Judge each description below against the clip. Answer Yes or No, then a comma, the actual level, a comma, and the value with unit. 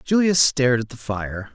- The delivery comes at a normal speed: Yes, average, 195 wpm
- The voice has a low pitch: Yes, low, 130 Hz